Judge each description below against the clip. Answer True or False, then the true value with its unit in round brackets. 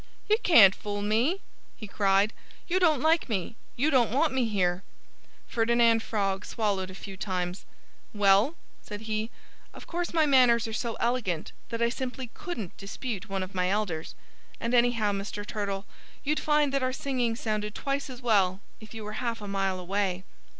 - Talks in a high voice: True (220 Hz)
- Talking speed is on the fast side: False (175 wpm)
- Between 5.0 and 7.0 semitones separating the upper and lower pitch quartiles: False (4.3 semitones)